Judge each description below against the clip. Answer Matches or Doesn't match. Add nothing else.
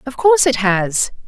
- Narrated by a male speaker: Doesn't match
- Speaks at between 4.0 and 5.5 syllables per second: Matches